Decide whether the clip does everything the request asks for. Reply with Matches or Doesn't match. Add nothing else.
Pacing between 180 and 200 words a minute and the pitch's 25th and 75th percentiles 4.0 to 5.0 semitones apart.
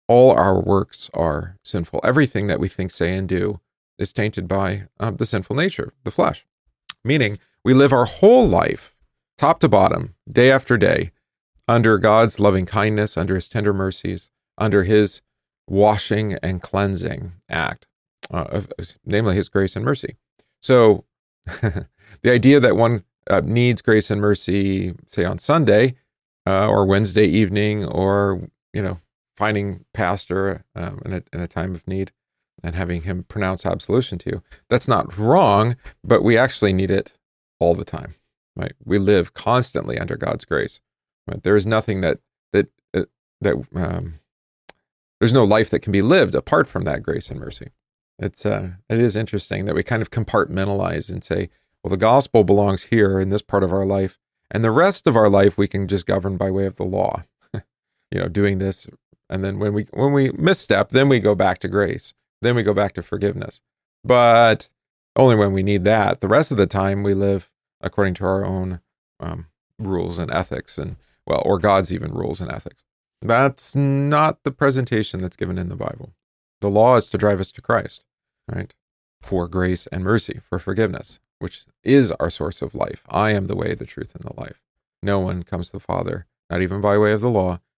Doesn't match